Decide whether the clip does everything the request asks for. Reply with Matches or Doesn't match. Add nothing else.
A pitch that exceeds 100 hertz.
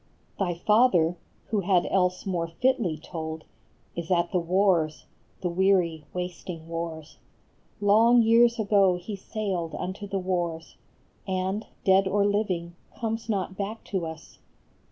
Matches